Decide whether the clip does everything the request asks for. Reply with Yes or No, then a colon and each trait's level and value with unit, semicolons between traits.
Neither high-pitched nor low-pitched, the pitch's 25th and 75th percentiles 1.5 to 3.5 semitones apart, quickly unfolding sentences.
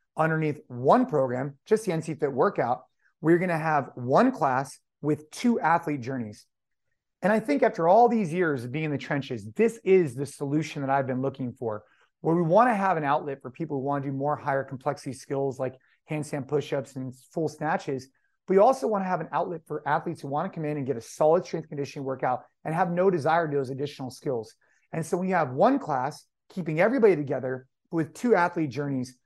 No: medium, 150 Hz; average, 4.1 semitones; fast, 220 wpm